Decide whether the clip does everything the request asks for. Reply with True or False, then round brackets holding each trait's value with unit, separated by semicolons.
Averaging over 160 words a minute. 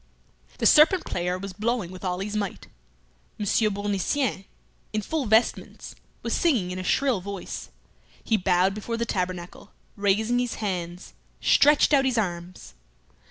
False (145 wpm)